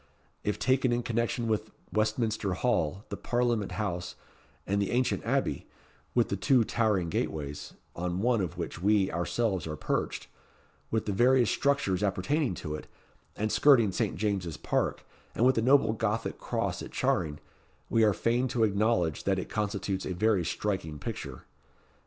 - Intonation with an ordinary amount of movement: Yes, average, 4.1 semitones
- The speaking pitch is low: Yes, low, 105 Hz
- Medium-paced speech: Yes, average, 160 wpm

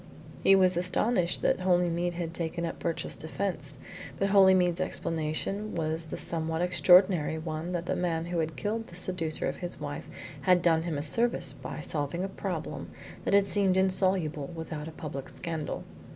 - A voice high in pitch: No, medium, 175 Hz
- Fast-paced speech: No, average, 170 wpm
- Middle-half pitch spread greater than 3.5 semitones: No, narrow, 2.5 semitones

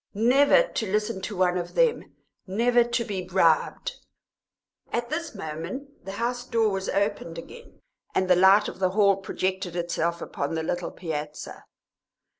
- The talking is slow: No, average, 160 wpm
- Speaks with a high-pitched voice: Yes, high, 195 Hz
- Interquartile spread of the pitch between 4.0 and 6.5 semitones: Yes, average, 5.0 semitones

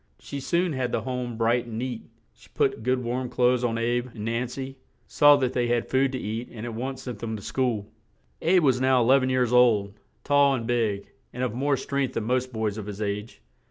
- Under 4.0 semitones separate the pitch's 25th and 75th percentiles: Yes, narrow, 2.4 semitones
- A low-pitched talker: Yes, low, 125 Hz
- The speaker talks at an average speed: No, fast, 230 wpm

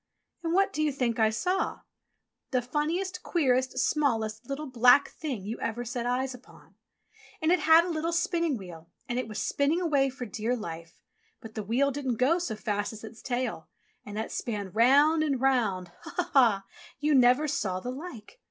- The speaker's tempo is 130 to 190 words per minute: No, average, 200 wpm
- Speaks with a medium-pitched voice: No, very high, 255 Hz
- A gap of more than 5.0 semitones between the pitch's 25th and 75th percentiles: Yes, wide, 5.5 semitones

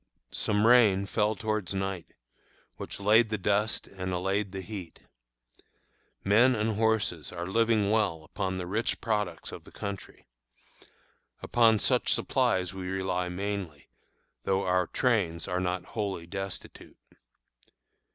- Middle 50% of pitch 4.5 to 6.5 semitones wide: No, average, 2.8 semitones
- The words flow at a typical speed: No, slow, 130 wpm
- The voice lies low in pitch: Yes, low, 100 Hz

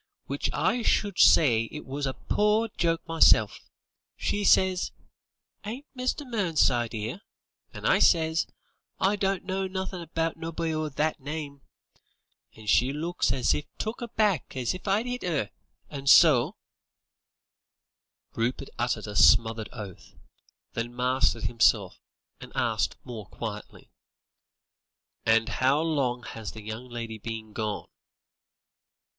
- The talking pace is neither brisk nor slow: No, slow, 130 wpm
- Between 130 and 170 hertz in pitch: Yes, medium, 140 Hz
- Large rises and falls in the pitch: Yes, wide, 8.0 semitones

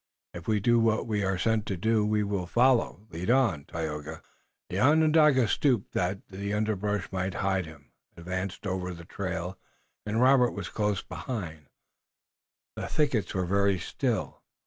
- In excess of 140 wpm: Yes, average, 155 wpm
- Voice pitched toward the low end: Yes, low, 100 Hz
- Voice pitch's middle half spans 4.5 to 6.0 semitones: No, average, 3.7 semitones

